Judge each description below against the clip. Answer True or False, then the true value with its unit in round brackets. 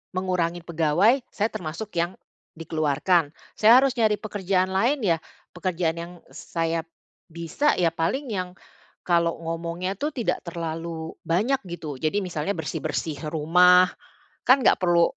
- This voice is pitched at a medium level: True (175 Hz)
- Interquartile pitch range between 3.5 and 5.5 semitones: False (2.8 semitones)